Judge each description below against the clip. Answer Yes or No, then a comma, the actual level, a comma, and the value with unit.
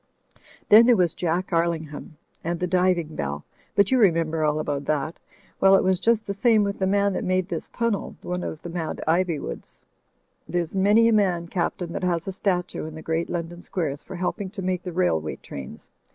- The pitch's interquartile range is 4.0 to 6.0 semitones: No, average, 3.1 semitones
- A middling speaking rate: No, fast, 210 wpm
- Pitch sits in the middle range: Yes, medium, 180 Hz